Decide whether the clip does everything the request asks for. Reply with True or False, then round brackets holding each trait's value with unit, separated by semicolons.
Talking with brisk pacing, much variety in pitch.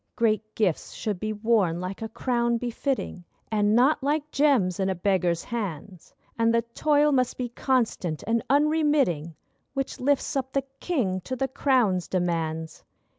False (155 wpm; 6.3 semitones)